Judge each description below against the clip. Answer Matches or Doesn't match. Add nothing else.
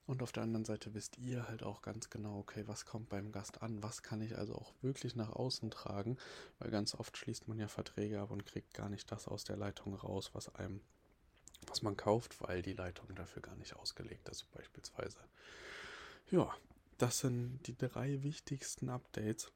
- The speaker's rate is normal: Doesn't match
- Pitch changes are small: Doesn't match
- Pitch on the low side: Matches